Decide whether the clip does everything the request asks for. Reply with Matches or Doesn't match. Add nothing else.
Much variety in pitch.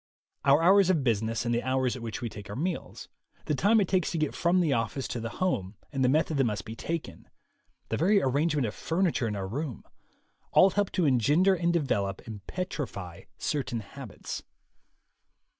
Matches